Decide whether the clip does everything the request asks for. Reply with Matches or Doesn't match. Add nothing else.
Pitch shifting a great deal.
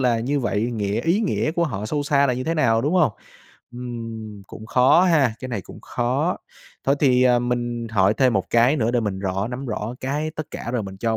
Doesn't match